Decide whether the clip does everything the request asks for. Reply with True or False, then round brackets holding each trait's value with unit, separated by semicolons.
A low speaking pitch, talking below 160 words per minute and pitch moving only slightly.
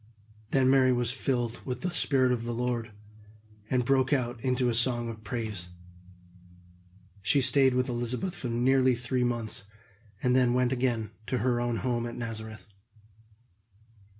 True (125 Hz; 150 wpm; 1.6 semitones)